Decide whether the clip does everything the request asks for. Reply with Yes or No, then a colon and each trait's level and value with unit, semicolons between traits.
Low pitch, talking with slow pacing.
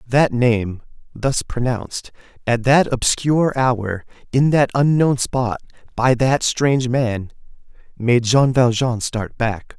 Yes: low, 125 Hz; slow, 130 wpm